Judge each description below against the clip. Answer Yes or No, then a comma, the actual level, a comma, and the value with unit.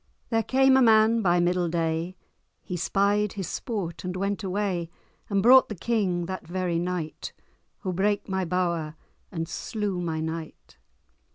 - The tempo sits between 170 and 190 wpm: No, average, 155 wpm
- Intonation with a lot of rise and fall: No, average, 3.3 semitones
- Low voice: No, medium, 185 Hz